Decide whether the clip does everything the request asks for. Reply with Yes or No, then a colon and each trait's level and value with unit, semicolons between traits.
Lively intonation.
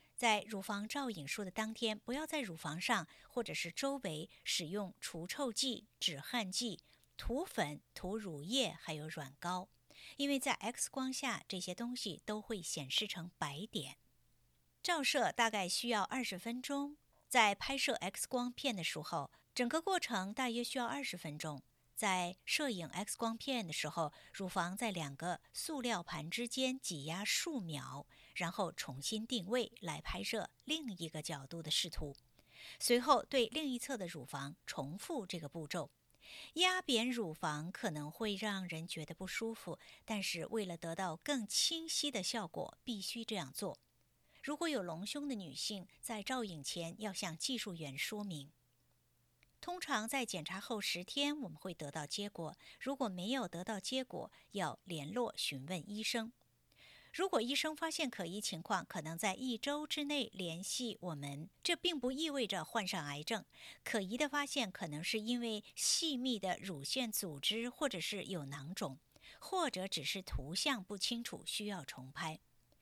Yes: wide, 6.9 semitones